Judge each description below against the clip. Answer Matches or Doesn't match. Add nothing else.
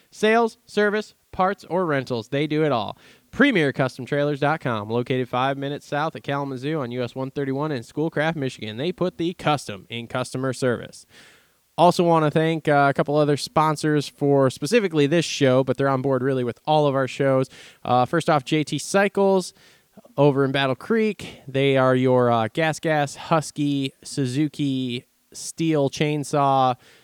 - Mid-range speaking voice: Matches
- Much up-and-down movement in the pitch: Doesn't match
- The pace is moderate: Matches